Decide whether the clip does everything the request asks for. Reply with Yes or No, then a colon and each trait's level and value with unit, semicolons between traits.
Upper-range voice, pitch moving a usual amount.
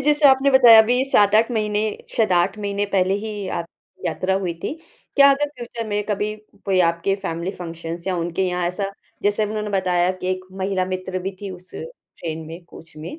Yes: high, 195 Hz; average, 3.5 semitones